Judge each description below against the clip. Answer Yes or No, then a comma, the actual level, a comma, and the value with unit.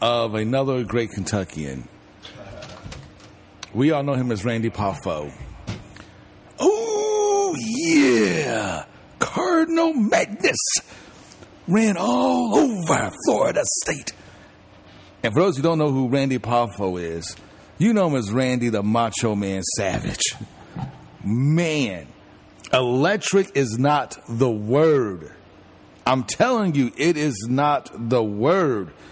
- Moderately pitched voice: No, low, 125 Hz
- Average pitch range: No, wide, 6.9 semitones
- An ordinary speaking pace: No, slow, 110 wpm